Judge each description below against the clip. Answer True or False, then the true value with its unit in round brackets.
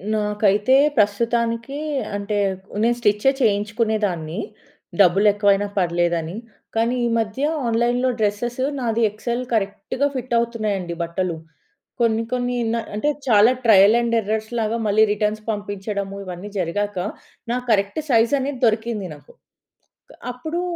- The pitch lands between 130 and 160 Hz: False (215 Hz)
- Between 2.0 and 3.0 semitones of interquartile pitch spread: True (2.7 semitones)